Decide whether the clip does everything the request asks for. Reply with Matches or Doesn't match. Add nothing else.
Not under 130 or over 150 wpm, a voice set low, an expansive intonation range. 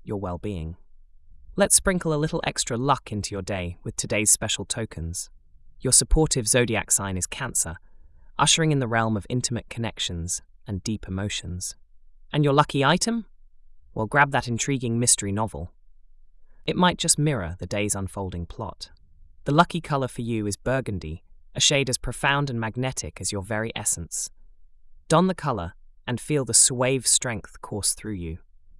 Doesn't match